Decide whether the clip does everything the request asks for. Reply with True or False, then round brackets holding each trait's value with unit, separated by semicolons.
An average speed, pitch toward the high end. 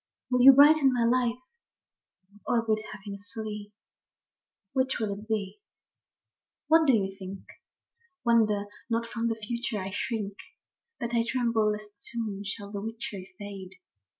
True (150 wpm; 220 Hz)